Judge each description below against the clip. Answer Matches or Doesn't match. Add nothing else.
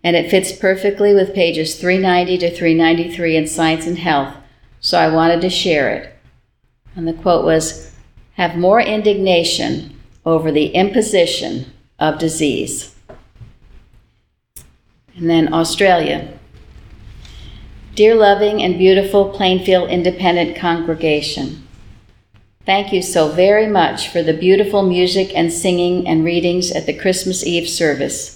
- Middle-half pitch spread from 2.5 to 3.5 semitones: Matches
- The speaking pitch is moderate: Matches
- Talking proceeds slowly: Matches